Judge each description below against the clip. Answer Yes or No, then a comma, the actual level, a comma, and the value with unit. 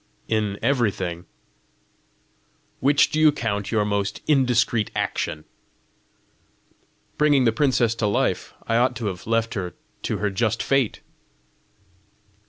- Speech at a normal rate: No, slow, 120 wpm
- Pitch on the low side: Yes, low, 115 Hz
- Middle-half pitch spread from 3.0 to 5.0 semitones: Yes, average, 3.7 semitones